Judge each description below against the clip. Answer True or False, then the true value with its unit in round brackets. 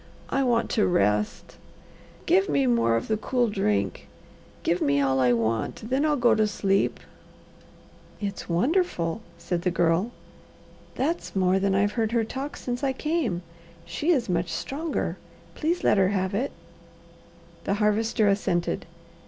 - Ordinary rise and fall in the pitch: False (6.3 semitones)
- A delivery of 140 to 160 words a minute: True (150 wpm)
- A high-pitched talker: True (200 Hz)